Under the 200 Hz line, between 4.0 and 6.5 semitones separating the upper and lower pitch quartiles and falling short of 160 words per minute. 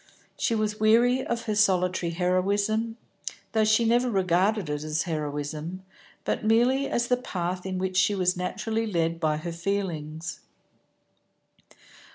Yes: high, 190 Hz; average, 4.5 semitones; average, 140 wpm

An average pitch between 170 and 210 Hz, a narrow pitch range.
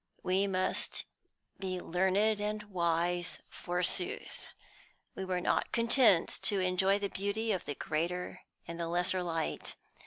Yes: medium, 185 Hz; narrow, 2.3 semitones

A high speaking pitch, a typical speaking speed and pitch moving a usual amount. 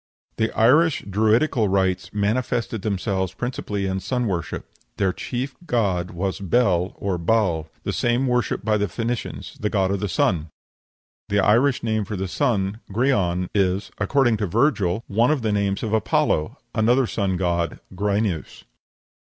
No: low, 105 Hz; average, 150 wpm; average, 3.7 semitones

